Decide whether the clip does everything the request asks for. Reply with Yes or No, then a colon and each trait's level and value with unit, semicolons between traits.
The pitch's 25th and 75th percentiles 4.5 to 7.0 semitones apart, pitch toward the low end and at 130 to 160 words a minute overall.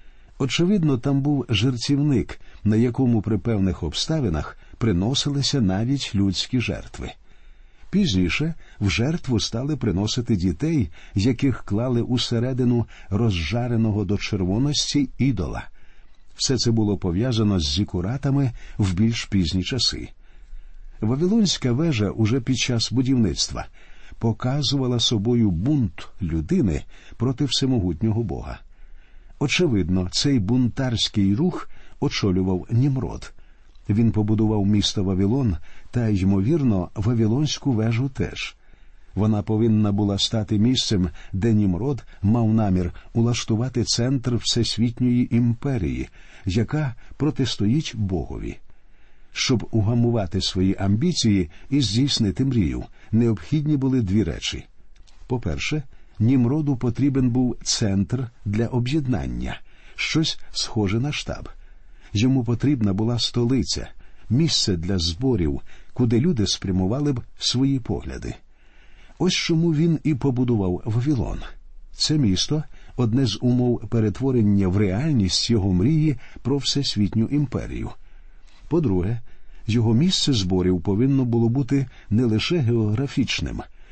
No: average, 5.0 semitones; low, 115 Hz; slow, 105 wpm